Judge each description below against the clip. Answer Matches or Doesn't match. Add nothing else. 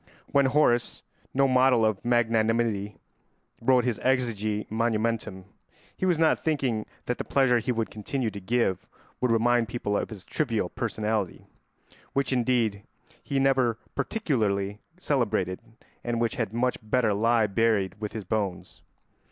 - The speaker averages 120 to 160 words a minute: Matches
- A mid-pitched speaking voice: Doesn't match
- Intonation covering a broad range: Doesn't match